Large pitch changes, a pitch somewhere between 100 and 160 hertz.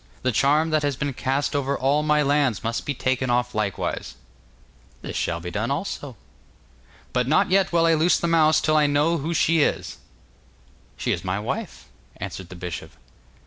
No: average, 4.0 semitones; medium, 140 Hz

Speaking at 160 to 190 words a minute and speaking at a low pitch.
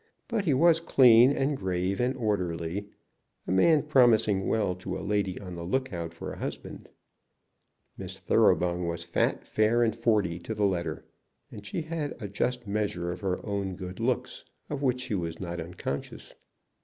Yes: average, 170 wpm; low, 100 Hz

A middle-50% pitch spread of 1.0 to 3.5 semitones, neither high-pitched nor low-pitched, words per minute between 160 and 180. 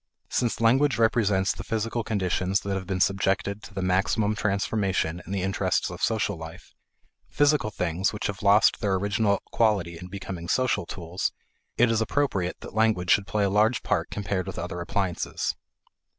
No: average, 2.9 semitones; low, 100 Hz; average, 170 wpm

